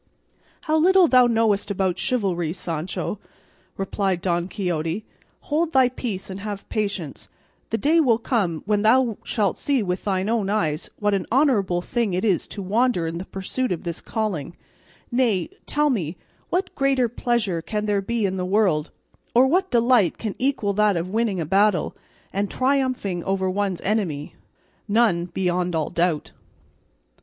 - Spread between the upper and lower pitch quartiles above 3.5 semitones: Yes, average, 4.8 semitones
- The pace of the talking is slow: No, average, 160 wpm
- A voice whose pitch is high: Yes, high, 205 Hz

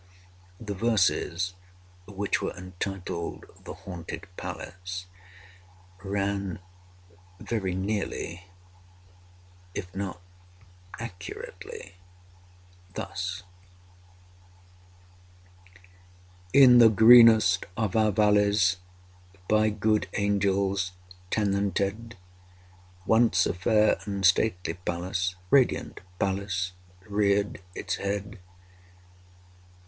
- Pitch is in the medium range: No, low, 100 Hz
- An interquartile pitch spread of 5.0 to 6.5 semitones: No, average, 2.7 semitones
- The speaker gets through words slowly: Yes, slow, 70 wpm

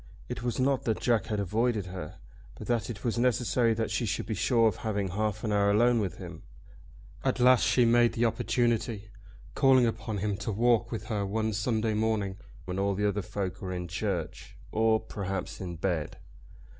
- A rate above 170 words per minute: Yes, average, 190 wpm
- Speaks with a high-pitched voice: No, low, 110 Hz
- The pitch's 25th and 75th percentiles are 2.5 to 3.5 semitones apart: Yes, average, 2.8 semitones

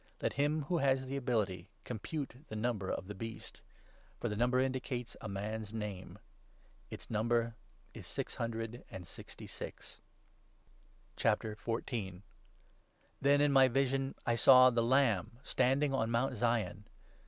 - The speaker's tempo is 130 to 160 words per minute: Yes, average, 140 wpm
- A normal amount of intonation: Yes, average, 3.7 semitones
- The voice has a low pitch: Yes, low, 120 Hz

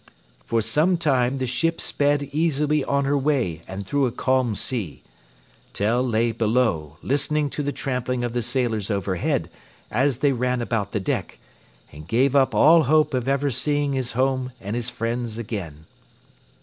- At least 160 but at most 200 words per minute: Yes, average, 165 wpm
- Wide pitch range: No, average, 3.7 semitones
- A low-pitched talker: Yes, low, 125 Hz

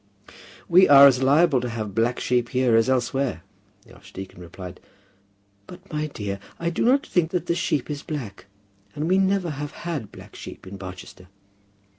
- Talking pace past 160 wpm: Yes, average, 175 wpm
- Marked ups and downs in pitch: Yes, wide, 7.0 semitones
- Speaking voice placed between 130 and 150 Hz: Yes, low, 135 Hz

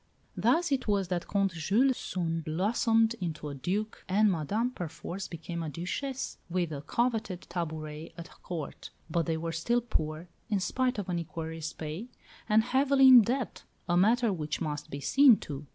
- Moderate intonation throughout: No, wide, 5.9 semitones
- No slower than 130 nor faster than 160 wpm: No, average, 170 wpm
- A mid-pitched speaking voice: Yes, medium, 180 Hz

